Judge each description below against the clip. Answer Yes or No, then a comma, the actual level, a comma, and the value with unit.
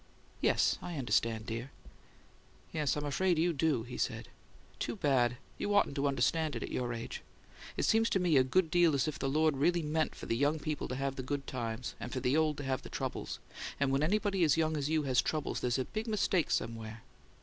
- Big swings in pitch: No, average, 3.9 semitones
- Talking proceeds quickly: Yes, fast, 225 wpm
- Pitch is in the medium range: Yes, medium, 145 Hz